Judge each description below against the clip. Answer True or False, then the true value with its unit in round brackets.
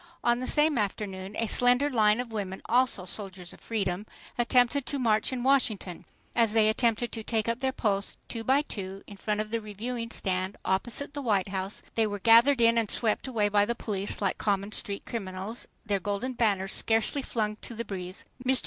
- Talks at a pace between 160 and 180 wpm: False (190 wpm)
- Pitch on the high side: True (220 Hz)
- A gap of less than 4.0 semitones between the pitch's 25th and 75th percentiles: True (3.2 semitones)